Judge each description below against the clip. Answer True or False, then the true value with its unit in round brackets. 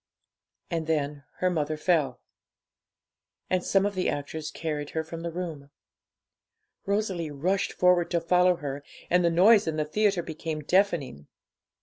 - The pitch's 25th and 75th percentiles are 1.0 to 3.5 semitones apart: True (3.1 semitones)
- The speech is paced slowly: False (145 wpm)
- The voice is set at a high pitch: False (165 Hz)